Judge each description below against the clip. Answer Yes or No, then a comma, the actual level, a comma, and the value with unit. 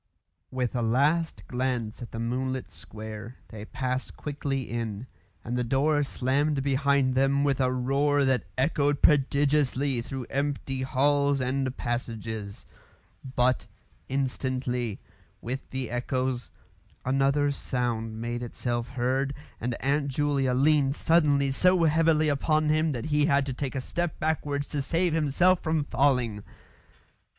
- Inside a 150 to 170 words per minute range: No, slow, 135 wpm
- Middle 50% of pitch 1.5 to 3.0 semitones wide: Yes, narrow, 2.6 semitones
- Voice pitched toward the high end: No, low, 135 Hz